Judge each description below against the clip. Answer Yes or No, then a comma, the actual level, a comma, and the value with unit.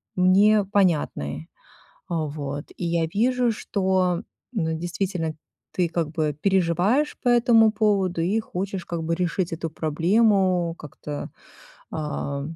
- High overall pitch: No, medium, 180 Hz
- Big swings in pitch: No, average, 3.8 semitones